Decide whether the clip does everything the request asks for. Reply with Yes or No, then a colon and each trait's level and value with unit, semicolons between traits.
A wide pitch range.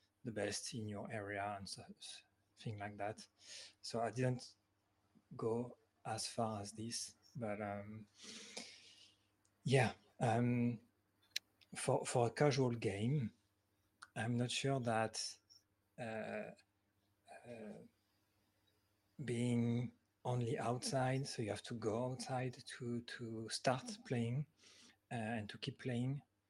No: average, 3.0 semitones